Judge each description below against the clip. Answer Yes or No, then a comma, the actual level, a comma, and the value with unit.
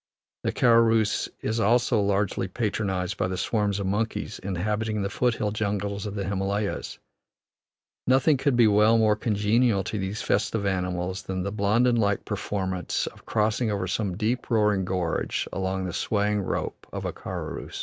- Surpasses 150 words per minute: Yes, average, 160 wpm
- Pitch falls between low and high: No, low, 105 Hz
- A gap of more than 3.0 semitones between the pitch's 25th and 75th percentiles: No, narrow, 2.5 semitones